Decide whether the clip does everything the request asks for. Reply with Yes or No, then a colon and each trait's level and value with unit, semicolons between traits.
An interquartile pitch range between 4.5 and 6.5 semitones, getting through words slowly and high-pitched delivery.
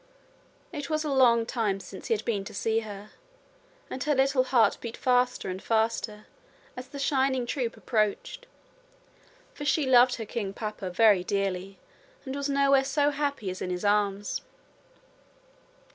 No: average, 4.9 semitones; average, 160 wpm; high, 235 Hz